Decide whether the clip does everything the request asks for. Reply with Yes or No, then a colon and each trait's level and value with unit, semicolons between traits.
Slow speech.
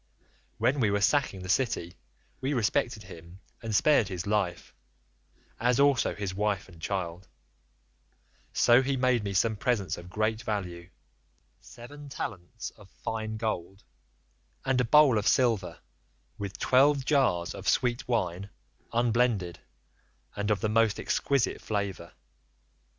Yes: slow, 130 wpm